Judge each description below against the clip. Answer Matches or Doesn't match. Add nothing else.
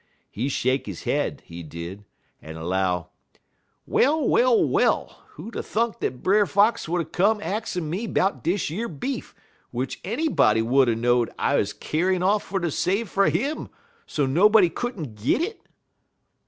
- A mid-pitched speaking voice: Matches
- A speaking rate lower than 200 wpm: Matches